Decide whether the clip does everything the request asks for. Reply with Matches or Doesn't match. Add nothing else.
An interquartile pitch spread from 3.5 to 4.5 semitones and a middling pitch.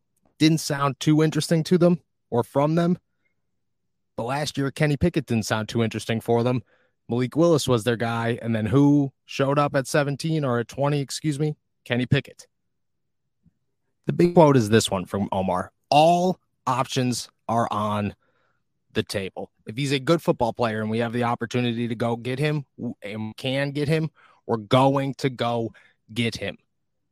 Doesn't match